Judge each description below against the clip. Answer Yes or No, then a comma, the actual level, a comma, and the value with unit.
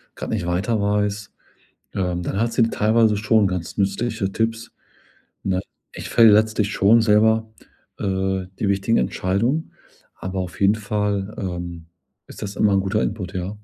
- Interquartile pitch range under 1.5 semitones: No, narrow, 2.5 semitones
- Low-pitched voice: Yes, low, 100 Hz